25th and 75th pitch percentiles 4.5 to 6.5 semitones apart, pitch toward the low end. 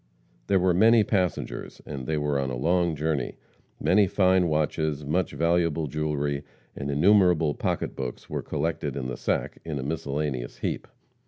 No: average, 3.8 semitones; very low, 75 Hz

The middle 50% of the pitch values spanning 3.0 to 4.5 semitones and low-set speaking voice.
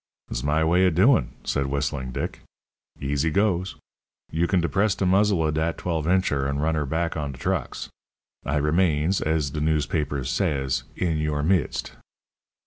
Yes: average, 3.7 semitones; very low, 80 Hz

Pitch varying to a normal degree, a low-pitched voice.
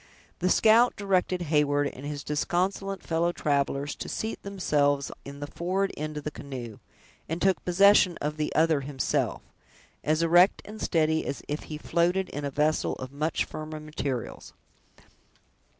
No: average, 3.8 semitones; medium, 155 Hz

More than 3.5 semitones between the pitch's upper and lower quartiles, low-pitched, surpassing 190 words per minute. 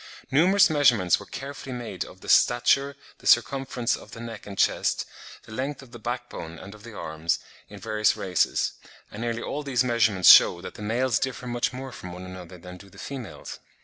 Yes: average, 5.1 semitones; low, 115 Hz; fast, 205 wpm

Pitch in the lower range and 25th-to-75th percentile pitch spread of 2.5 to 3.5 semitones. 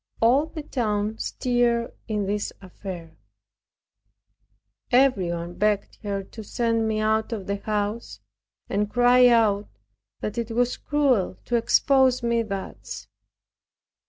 No: high, 220 Hz; average, 3.2 semitones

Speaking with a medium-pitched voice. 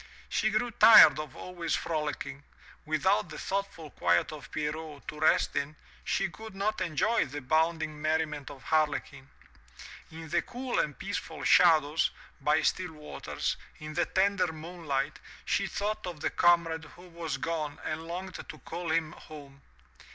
Yes: medium, 160 Hz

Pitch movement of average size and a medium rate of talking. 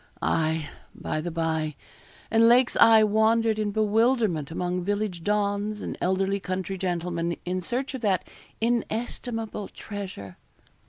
No: average, 4.1 semitones; slow, 125 wpm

